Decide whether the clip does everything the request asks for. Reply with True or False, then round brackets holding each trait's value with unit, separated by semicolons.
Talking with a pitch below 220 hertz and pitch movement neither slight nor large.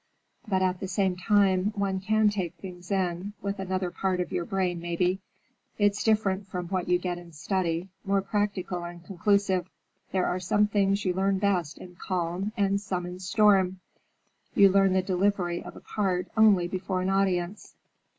False (190 Hz; 1.9 semitones)